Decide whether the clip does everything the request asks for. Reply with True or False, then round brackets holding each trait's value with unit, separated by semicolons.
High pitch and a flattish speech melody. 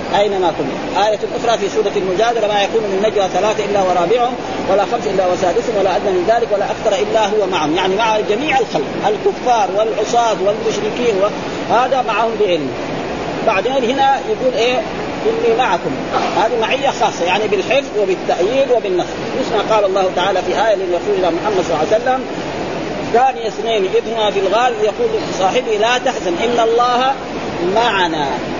False (220 Hz; 3.4 semitones)